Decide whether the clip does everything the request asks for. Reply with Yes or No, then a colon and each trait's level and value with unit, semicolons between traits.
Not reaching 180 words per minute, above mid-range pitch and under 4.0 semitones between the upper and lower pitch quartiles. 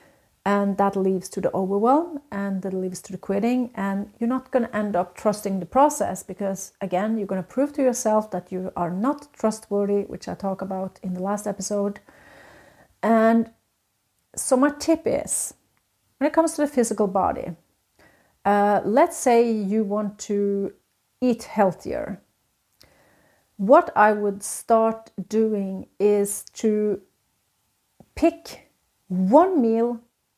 Yes: average, 145 wpm; high, 210 Hz; average, 3.5 semitones